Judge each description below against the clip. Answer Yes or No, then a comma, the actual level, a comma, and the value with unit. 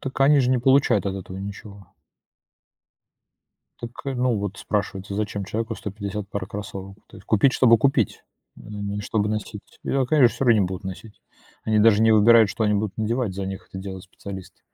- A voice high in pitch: No, low, 105 Hz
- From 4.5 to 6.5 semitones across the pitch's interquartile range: No, average, 2.9 semitones